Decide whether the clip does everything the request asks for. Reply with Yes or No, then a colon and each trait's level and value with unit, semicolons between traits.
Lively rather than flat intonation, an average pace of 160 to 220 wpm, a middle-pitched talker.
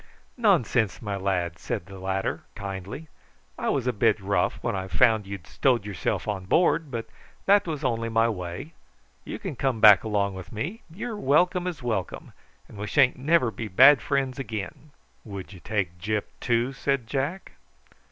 No: wide, 5.9 semitones; average, 170 wpm; low, 115 Hz